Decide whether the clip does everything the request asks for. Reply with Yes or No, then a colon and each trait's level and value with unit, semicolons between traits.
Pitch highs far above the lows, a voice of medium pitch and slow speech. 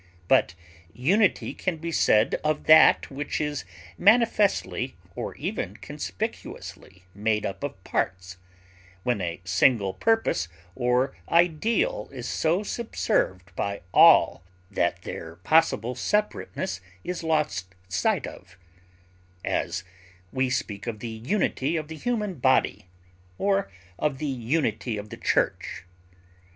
No: wide, 8.9 semitones; low, 130 Hz; slow, 120 wpm